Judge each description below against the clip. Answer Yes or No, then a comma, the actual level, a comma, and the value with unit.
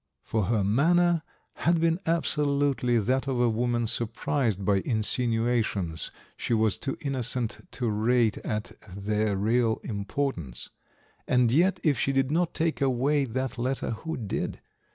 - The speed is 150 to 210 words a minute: No, average, 140 wpm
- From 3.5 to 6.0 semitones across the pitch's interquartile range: Yes, average, 4.3 semitones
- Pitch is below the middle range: Yes, low, 120 Hz